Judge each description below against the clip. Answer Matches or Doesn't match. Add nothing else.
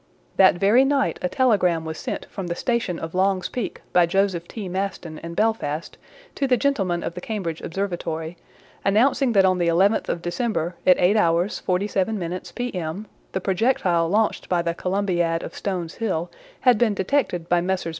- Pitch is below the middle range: Doesn't match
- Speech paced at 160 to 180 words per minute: Matches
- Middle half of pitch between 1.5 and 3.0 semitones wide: Doesn't match